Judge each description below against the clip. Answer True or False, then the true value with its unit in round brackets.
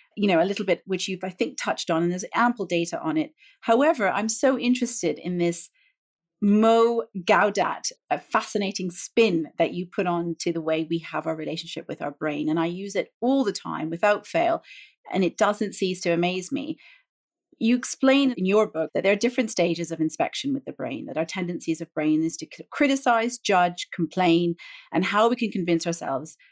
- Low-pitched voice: False (190 Hz)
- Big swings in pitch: True (5.7 semitones)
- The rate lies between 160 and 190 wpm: False (200 wpm)